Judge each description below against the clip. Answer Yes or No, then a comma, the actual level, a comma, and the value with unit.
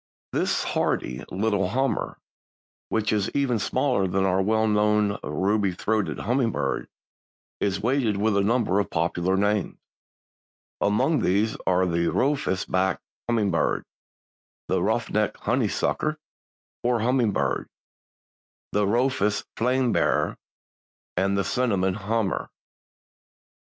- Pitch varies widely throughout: No, average, 3.5 semitones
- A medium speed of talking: No, slow, 115 wpm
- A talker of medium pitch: No, low, 105 Hz